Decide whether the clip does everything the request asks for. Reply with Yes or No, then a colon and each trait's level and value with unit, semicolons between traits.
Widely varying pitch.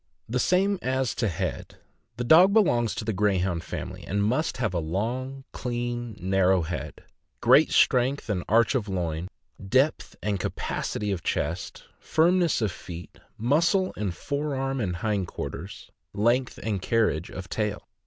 Yes: wide, 5.7 semitones